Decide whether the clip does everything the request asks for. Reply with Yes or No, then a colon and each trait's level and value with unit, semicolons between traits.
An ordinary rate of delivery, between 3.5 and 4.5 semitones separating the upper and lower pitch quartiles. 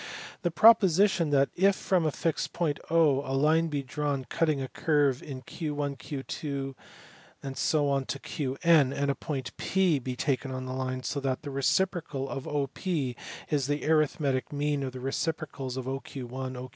No: average, 160 wpm; average, 2.8 semitones